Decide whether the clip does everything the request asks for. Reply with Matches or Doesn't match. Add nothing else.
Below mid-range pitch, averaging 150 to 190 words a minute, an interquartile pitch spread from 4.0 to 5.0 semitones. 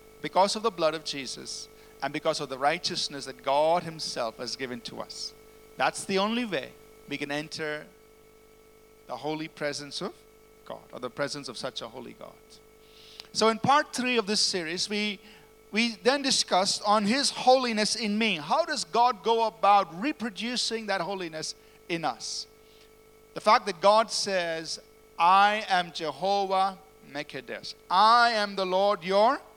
Doesn't match